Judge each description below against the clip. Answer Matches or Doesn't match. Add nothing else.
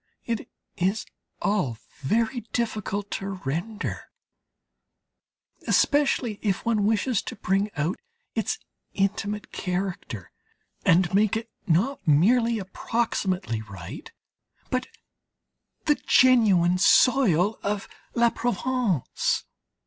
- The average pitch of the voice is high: Matches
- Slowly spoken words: Matches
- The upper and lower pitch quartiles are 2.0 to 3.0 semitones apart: Doesn't match